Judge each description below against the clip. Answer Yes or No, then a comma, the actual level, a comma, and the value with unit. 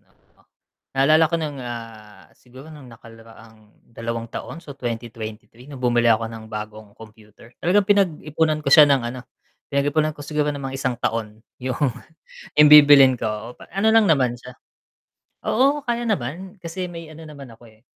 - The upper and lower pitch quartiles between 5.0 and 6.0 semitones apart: Yes, average, 5.3 semitones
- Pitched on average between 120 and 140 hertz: Yes, low, 135 Hz